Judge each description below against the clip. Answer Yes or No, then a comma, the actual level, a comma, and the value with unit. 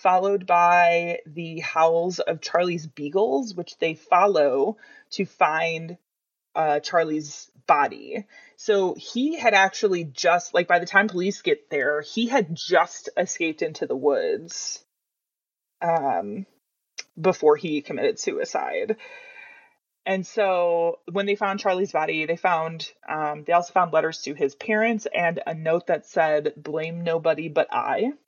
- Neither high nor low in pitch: Yes, medium, 175 Hz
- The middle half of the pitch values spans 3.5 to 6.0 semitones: Yes, average, 4.2 semitones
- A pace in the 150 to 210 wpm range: No, average, 140 wpm